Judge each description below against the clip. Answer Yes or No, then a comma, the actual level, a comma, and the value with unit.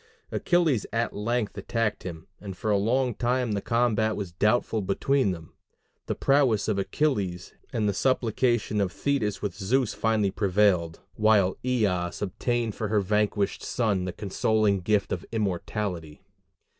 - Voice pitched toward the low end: Yes, low, 105 Hz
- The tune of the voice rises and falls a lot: No, average, 3.3 semitones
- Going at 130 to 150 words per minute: Yes, average, 145 wpm